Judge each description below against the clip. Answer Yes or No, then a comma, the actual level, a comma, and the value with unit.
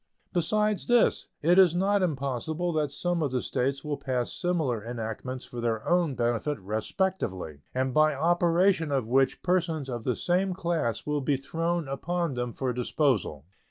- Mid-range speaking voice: Yes, medium, 145 Hz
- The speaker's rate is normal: Yes, average, 160 wpm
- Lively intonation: Yes, wide, 5.9 semitones